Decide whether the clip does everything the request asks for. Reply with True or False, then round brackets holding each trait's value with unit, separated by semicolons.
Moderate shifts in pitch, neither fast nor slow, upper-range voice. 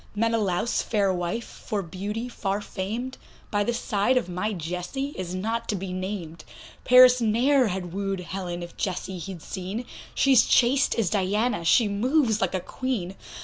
True (4.2 semitones; 160 wpm; 205 Hz)